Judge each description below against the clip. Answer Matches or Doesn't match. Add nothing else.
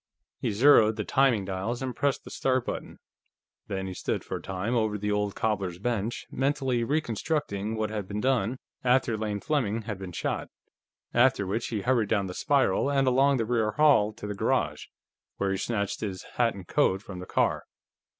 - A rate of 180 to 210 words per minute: Matches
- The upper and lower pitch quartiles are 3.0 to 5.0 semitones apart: Matches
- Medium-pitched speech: Doesn't match